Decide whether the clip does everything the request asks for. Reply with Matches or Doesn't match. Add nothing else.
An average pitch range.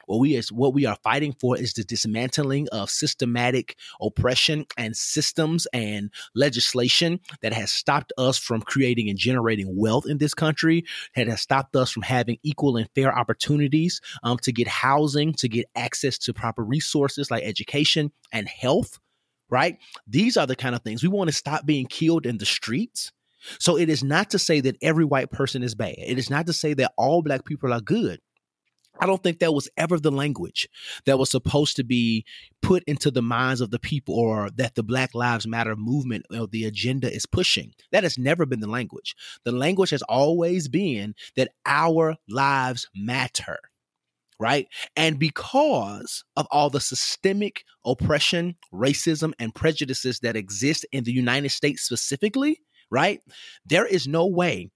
Matches